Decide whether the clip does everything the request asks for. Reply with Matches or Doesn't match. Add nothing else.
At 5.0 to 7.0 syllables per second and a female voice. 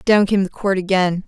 Matches